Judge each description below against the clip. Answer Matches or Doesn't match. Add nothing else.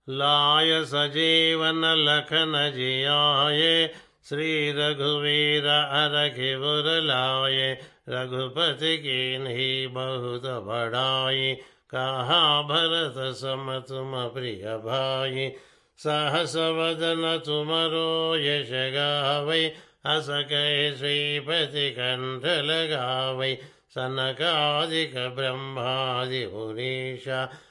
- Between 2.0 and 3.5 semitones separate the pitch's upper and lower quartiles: Matches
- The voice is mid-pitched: Matches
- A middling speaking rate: Doesn't match